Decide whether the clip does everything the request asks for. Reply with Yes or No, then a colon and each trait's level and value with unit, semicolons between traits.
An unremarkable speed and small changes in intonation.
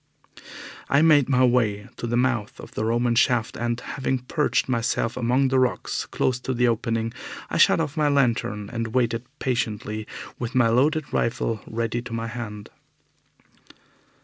Yes: average, 160 wpm; narrow, 2.2 semitones